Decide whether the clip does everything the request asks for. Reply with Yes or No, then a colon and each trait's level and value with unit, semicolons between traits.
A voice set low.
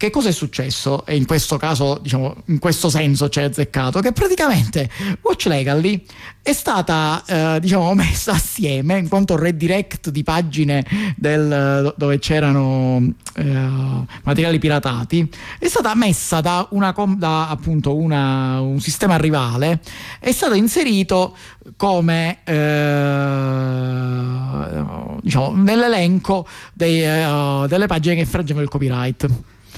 No: medium, 155 Hz